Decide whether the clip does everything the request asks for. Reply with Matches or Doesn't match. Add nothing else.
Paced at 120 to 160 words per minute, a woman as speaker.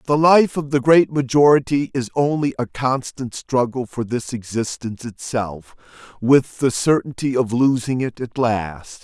Doesn't match